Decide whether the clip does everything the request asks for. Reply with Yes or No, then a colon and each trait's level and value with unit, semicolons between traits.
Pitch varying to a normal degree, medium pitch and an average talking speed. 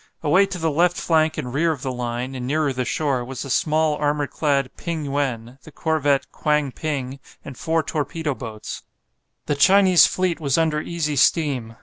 Yes: average, 3.3 semitones; medium, 145 Hz; average, 185 wpm